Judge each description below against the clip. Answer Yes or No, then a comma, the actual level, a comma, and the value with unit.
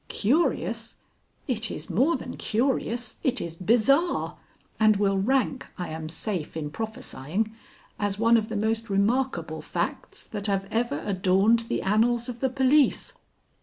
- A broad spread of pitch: No, average, 3.8 semitones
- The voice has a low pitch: No, high, 220 Hz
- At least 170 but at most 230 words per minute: No, average, 145 wpm